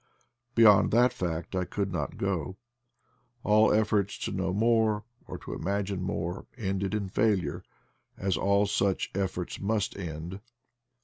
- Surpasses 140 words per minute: No, slow, 135 wpm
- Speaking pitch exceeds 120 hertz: No, low, 100 Hz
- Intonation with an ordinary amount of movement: No, narrow, 2.1 semitones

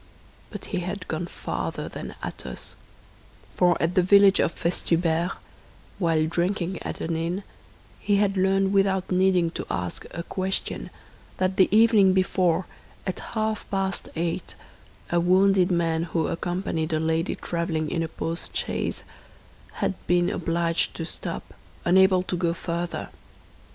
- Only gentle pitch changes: Yes, narrow, 2.3 semitones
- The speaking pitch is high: No, medium, 180 Hz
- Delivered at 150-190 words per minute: No, average, 140 wpm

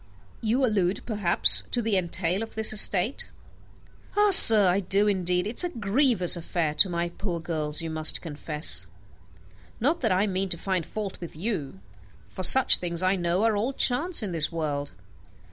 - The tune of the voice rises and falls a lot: No, average, 4.3 semitones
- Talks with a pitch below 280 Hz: Yes, medium, 185 Hz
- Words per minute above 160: Yes, average, 180 wpm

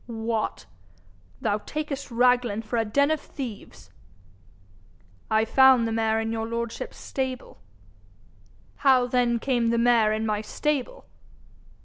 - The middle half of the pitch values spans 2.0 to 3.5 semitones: Yes, average, 2.7 semitones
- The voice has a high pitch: Yes, high, 235 Hz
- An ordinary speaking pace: No, slow, 125 wpm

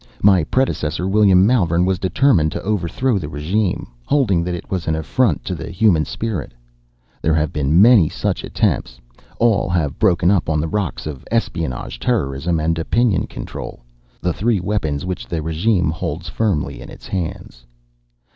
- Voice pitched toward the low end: Yes, very low, 90 Hz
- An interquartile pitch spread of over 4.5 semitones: Yes, average, 4.9 semitones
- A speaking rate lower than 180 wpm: Yes, average, 160 wpm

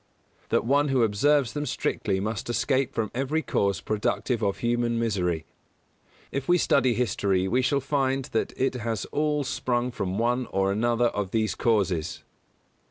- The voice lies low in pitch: Yes, low, 120 Hz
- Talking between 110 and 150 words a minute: No, average, 160 wpm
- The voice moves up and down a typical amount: Yes, average, 4.5 semitones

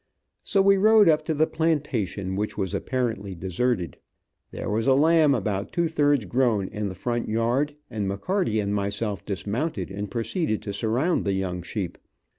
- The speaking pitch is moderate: No, low, 115 Hz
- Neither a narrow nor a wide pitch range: No, wide, 7.0 semitones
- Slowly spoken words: No, average, 170 wpm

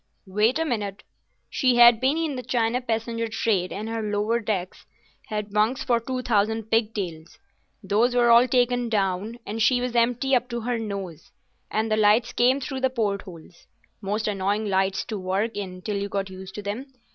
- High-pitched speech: Yes, high, 220 Hz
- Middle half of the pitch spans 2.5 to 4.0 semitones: Yes, average, 3.2 semitones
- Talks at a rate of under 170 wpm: No, average, 185 wpm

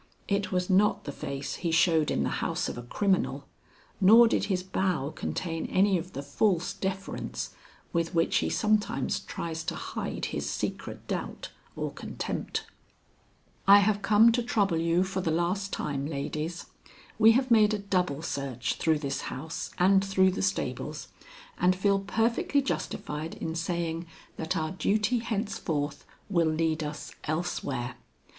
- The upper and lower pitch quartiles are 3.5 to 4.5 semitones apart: Yes, average, 4.0 semitones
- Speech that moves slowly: No, average, 155 wpm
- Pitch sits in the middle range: Yes, medium, 180 Hz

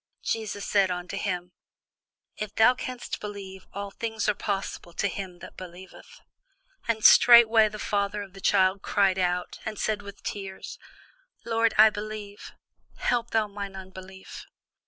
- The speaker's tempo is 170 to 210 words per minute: No, average, 145 wpm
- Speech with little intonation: Yes, narrow, 2.3 semitones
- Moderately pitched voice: No, high, 200 Hz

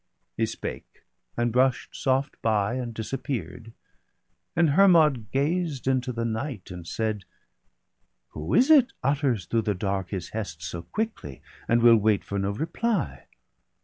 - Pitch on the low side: Yes, low, 115 Hz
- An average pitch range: No, wide, 5.7 semitones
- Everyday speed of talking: Yes, average, 150 wpm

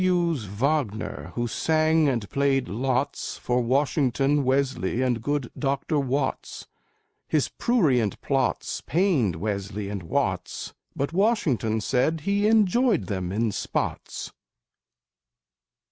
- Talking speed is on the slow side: Yes, slow, 110 wpm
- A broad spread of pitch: Yes, wide, 5.9 semitones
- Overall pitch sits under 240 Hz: Yes, low, 135 Hz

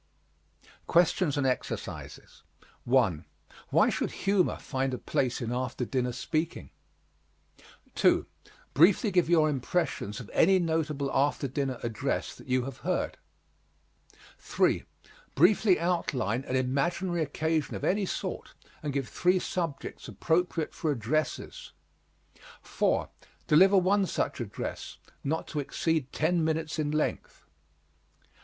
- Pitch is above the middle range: No, medium, 150 Hz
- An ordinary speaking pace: No, slow, 120 wpm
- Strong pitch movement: No, average, 4.8 semitones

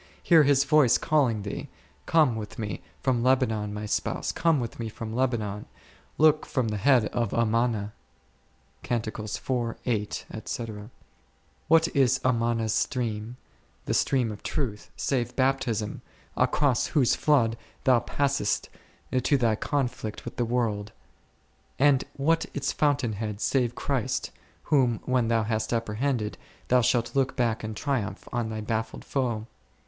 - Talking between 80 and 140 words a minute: Yes, slow, 135 wpm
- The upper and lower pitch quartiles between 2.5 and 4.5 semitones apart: Yes, average, 3.5 semitones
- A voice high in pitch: No, low, 120 Hz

